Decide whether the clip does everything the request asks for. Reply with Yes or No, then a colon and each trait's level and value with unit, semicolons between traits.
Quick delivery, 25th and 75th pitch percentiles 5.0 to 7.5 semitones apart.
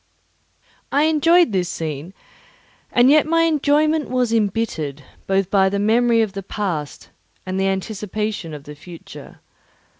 No: average, 140 wpm; wide, 5.6 semitones